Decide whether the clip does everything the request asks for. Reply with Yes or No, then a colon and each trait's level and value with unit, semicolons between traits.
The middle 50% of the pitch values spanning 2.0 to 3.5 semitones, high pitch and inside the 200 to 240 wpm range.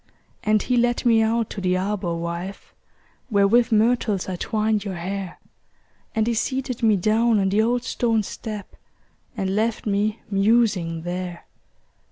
No: average, 3.1 semitones; high, 210 Hz; average, 155 wpm